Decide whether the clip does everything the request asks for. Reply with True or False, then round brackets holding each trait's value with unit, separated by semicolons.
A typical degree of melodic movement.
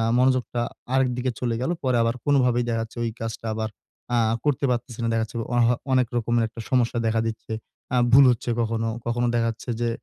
False (1.7 semitones)